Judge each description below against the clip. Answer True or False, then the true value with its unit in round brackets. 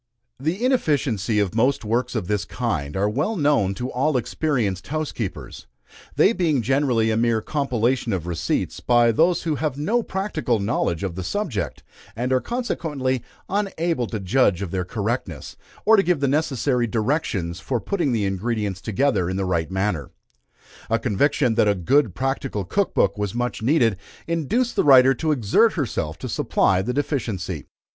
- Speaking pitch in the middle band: False (120 Hz)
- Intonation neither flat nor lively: False (6.6 semitones)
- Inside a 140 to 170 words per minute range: True (165 wpm)